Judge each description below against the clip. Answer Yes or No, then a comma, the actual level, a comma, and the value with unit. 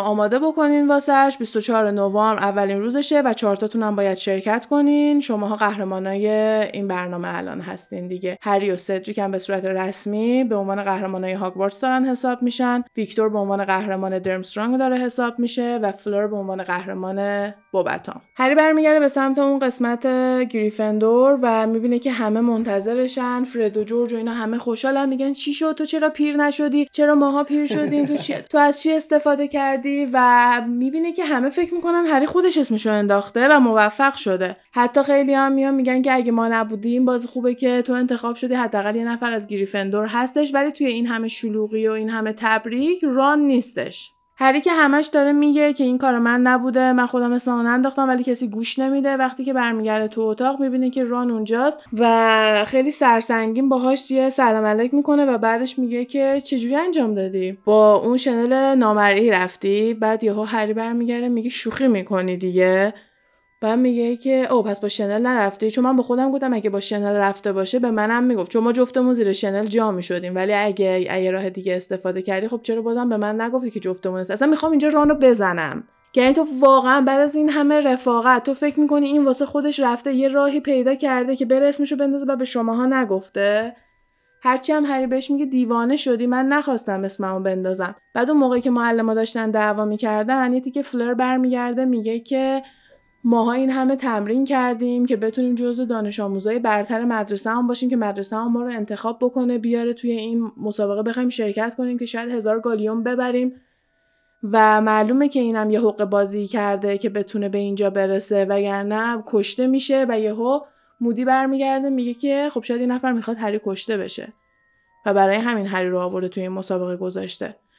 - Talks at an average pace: No, fast, 185 wpm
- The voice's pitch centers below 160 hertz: No, high, 235 Hz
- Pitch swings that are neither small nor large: Yes, average, 4.0 semitones